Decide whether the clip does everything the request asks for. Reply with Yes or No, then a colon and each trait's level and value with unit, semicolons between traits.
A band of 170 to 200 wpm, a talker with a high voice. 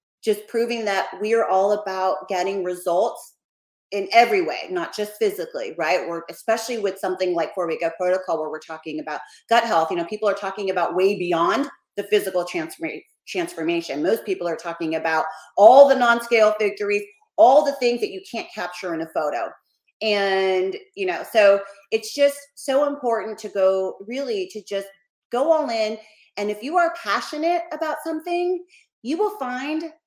Yes: average, 175 wpm; high, 220 Hz